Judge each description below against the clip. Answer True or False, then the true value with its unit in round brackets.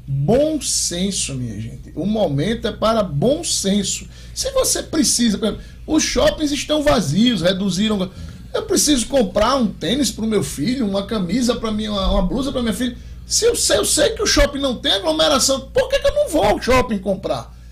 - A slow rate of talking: False (185 wpm)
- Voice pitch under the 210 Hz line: False (230 Hz)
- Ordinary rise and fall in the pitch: False (6.3 semitones)